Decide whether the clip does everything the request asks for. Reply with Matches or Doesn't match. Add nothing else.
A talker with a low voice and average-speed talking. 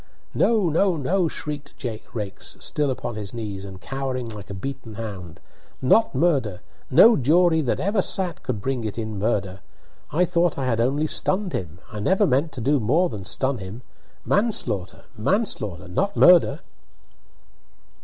Matches